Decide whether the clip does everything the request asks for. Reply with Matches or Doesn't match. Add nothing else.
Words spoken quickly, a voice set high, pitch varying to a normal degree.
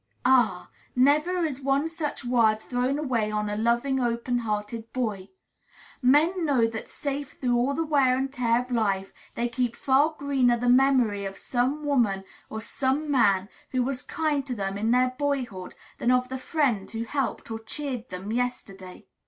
Doesn't match